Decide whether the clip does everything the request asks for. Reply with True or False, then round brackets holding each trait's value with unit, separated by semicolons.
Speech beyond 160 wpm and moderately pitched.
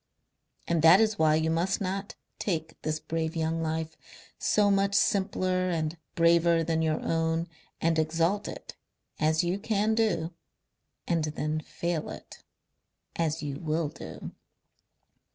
False (135 wpm; 165 Hz)